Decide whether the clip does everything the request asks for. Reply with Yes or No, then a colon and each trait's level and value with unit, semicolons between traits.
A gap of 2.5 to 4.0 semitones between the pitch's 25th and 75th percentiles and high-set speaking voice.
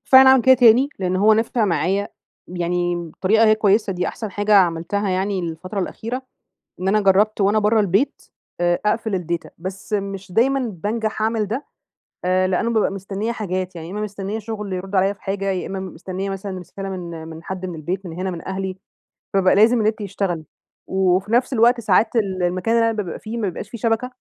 Yes: average, 2.9 semitones; high, 195 Hz